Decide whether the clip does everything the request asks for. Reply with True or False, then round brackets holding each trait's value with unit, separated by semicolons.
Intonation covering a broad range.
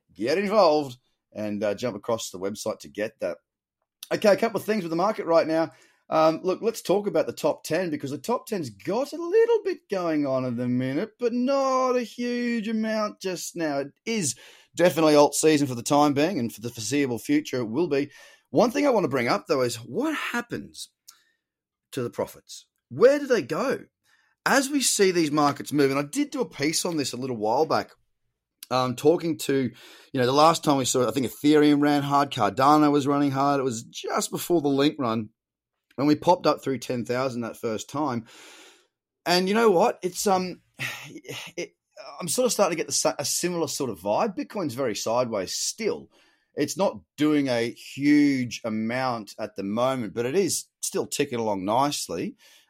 True (7.3 semitones)